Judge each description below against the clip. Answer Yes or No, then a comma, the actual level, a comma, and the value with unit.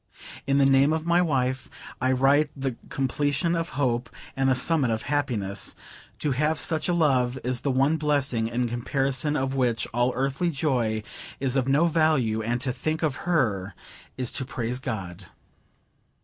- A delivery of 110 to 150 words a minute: No, average, 170 wpm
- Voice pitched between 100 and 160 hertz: Yes, low, 135 Hz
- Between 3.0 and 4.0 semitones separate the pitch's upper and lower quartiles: Yes, average, 3.3 semitones